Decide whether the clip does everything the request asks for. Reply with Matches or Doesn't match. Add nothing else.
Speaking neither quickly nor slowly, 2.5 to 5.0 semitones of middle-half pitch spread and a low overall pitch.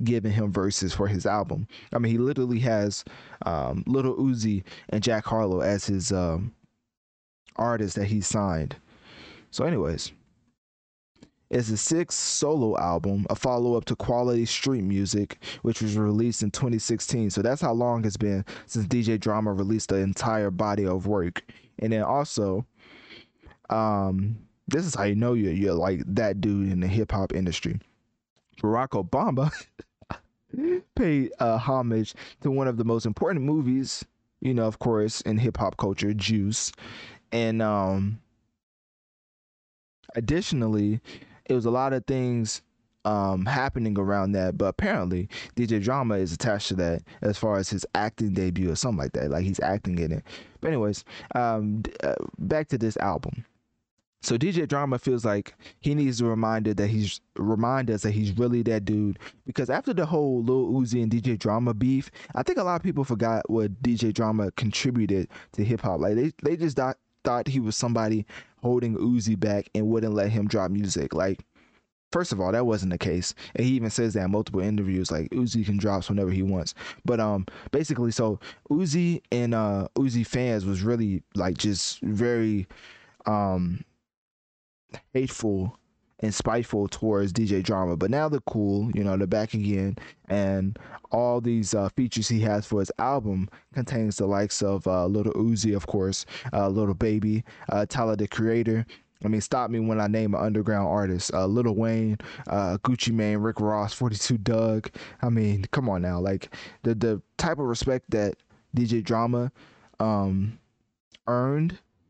Matches